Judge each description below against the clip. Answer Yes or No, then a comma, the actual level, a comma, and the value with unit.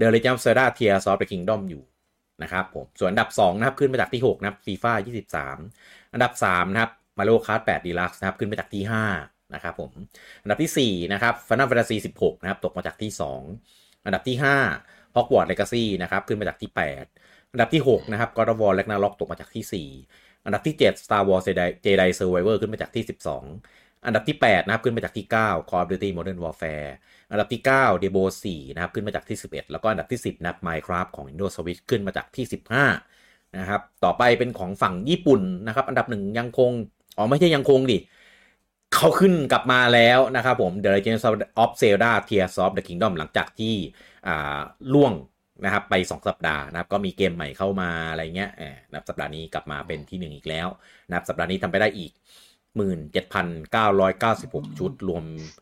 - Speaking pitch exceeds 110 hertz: No, low, 100 Hz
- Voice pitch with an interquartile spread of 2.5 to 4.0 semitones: No, average, 4.7 semitones